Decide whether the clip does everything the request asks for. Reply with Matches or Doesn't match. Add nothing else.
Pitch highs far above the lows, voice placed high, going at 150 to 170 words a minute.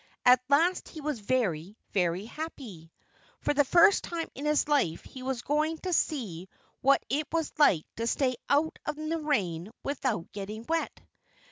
Matches